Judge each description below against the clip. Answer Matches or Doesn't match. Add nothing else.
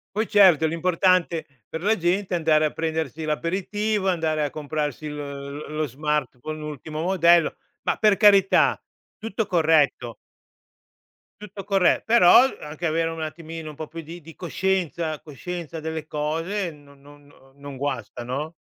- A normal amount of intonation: Matches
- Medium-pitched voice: Matches